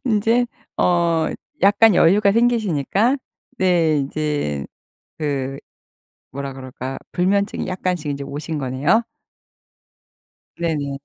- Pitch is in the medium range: Yes, medium, 165 Hz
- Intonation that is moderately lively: No, wide, 6.2 semitones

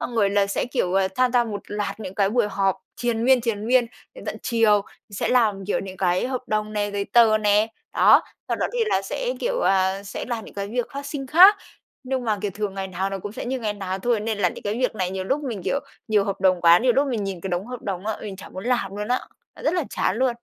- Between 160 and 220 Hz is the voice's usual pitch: Yes, high, 210 Hz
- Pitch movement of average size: Yes, average, 4.0 semitones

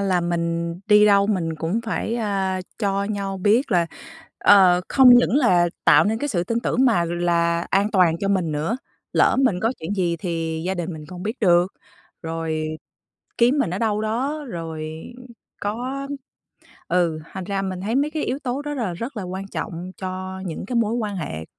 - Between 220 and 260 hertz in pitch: No, high, 190 Hz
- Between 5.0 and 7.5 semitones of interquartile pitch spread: No, average, 4.6 semitones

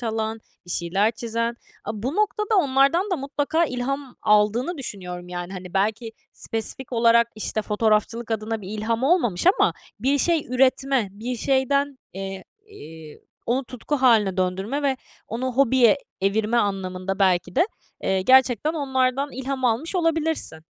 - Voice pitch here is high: Yes, high, 235 Hz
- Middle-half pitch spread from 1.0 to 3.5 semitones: No, average, 4.8 semitones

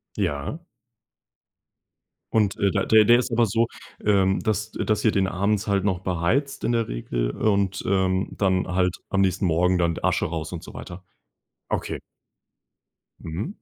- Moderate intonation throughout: Yes, average, 3.0 semitones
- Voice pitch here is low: Yes, very low, 95 Hz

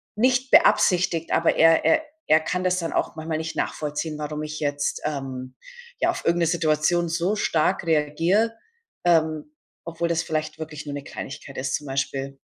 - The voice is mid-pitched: Yes, medium, 160 Hz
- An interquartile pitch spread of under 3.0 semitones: Yes, narrow, 2.4 semitones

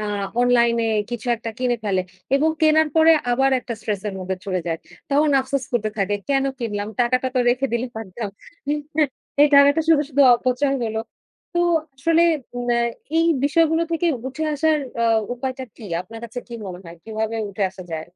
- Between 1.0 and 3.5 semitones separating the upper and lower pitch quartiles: No, average, 4.7 semitones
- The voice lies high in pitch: Yes, high, 245 Hz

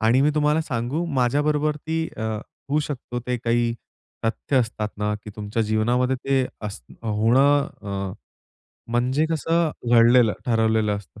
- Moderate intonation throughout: Yes, average, 4.6 semitones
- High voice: No, low, 120 Hz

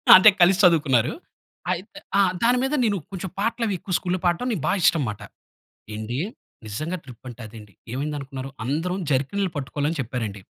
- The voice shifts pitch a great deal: Yes, wide, 6.8 semitones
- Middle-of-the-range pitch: Yes, medium, 150 Hz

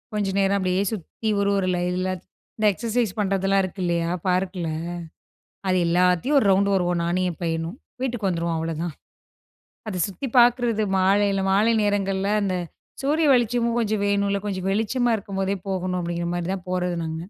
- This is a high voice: Yes, high, 195 Hz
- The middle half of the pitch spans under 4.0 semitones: Yes, average, 2.7 semitones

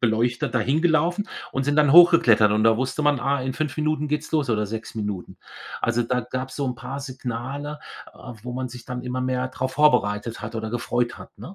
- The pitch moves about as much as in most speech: Yes, average, 3.7 semitones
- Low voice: Yes, low, 130 Hz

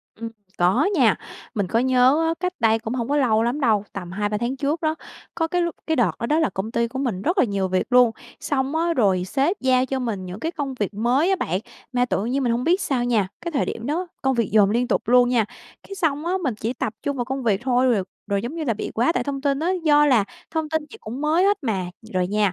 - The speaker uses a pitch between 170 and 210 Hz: No, very high, 250 Hz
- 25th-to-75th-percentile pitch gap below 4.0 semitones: No, average, 5.3 semitones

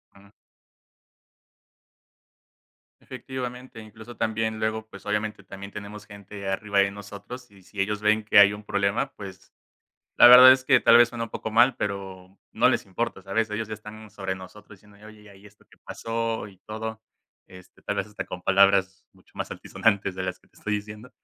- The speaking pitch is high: No, low, 105 Hz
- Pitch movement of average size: No, narrow, 2.0 semitones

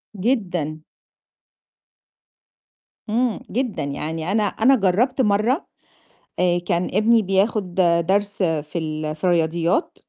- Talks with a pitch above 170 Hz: Yes, high, 190 Hz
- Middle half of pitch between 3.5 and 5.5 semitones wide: Yes, average, 4.9 semitones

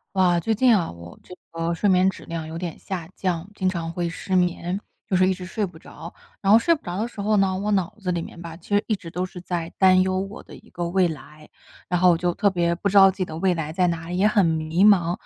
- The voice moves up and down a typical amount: No, narrow, 2.3 semitones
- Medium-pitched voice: Yes, medium, 180 Hz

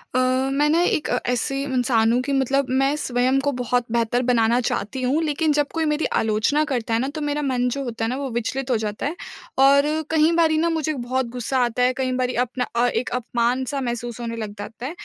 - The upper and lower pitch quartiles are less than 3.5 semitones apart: Yes, average, 2.9 semitones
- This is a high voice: Yes, very high, 255 Hz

